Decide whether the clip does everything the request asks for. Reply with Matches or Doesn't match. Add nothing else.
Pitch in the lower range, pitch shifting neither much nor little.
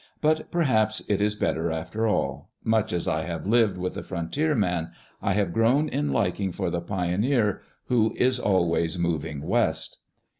Matches